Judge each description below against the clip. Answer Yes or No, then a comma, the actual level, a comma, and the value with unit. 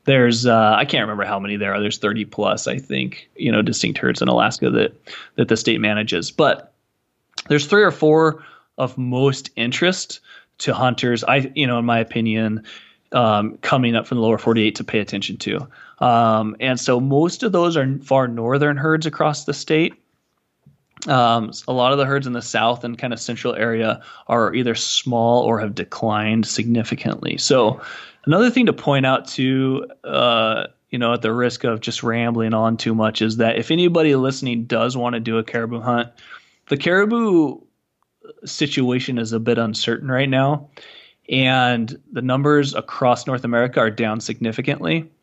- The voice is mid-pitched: No, low, 120 Hz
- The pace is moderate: Yes, average, 180 wpm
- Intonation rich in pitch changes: No, average, 3.4 semitones